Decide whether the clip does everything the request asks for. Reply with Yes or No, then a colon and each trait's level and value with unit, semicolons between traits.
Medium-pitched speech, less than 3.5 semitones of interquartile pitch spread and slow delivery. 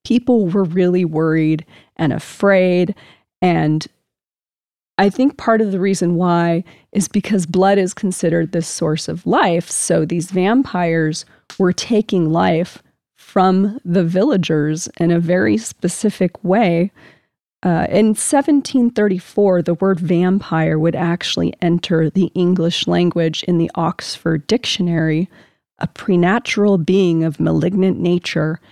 Yes: medium, 180 Hz; average, 2.7 semitones; slow, 125 wpm